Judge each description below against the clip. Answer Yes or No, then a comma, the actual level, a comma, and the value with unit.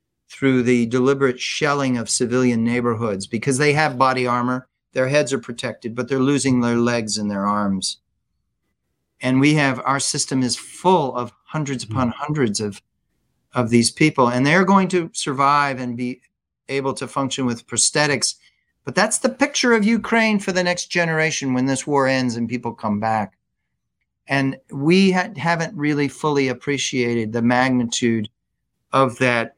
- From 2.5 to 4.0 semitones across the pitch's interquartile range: Yes, average, 3.6 semitones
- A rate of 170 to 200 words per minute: No, average, 160 wpm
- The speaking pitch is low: Yes, low, 130 Hz